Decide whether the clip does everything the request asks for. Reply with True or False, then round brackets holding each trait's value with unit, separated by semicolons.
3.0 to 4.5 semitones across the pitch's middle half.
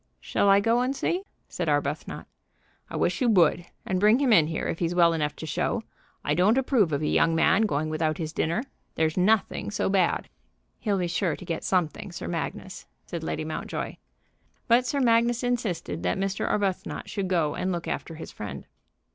False (5.2 semitones)